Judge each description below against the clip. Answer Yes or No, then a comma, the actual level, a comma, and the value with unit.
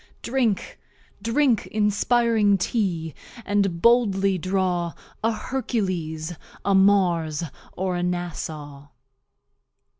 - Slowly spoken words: Yes, slow, 85 wpm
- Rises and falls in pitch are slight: No, average, 4.1 semitones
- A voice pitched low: No, high, 190 Hz